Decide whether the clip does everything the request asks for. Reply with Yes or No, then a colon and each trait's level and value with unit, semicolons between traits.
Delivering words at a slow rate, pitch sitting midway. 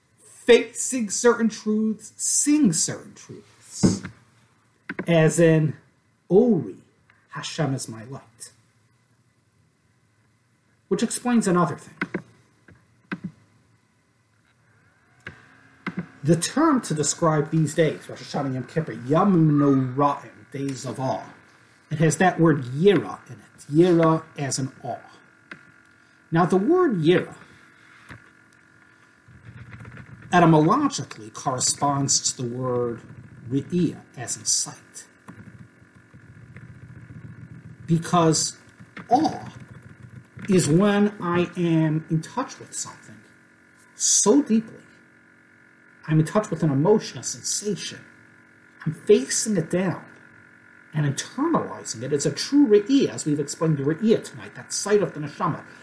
Yes: slow, 105 wpm; medium, 145 Hz